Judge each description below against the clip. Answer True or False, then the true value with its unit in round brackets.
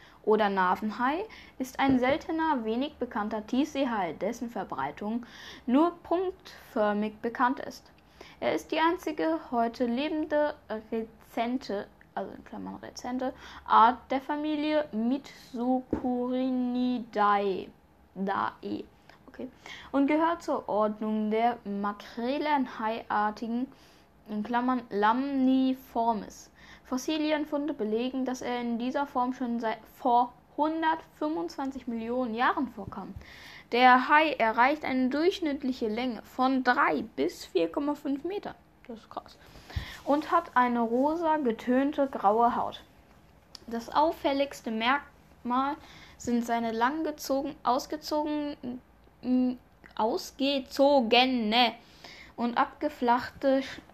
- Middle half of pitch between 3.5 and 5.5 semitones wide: True (3.9 semitones)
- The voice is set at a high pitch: True (255 Hz)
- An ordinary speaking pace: False (95 wpm)